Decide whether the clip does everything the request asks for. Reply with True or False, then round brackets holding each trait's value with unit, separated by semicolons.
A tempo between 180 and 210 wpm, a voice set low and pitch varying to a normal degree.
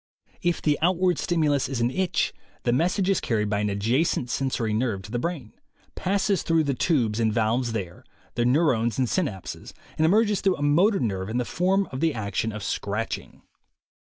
False (190 wpm; 130 Hz; 7.5 semitones)